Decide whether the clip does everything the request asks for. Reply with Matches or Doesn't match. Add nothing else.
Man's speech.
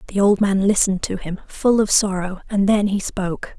Doesn't match